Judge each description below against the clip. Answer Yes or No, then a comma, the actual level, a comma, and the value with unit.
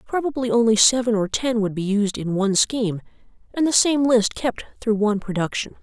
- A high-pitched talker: Yes, high, 225 Hz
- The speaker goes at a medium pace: Yes, average, 195 wpm